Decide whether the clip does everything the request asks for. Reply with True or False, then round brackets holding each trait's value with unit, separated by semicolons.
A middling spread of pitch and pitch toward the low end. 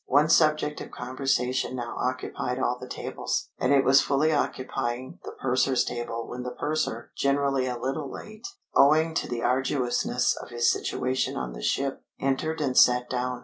False (2.3 semitones; 130 Hz)